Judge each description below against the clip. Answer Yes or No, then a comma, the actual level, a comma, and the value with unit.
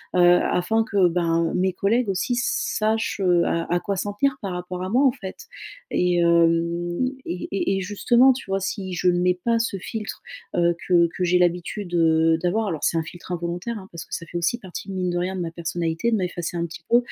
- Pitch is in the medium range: Yes, medium, 180 Hz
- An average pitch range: Yes, average, 3.0 semitones